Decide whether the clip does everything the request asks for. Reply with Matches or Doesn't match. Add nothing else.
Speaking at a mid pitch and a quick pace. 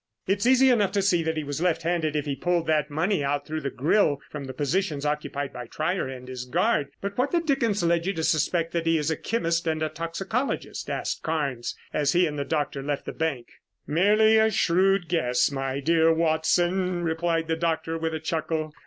Matches